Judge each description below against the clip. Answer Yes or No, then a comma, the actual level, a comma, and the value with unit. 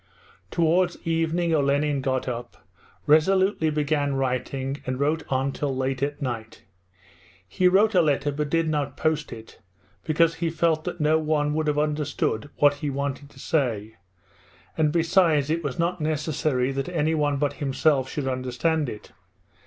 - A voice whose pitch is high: No, medium, 150 Hz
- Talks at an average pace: Yes, average, 155 wpm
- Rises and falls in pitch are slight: No, average, 3.0 semitones